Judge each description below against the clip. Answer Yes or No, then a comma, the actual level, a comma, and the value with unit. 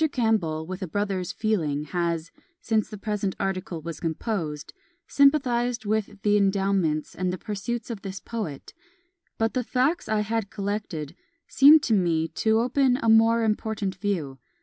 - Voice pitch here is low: No, high, 205 Hz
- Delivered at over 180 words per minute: No, average, 150 wpm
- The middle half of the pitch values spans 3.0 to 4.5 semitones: Yes, average, 4.2 semitones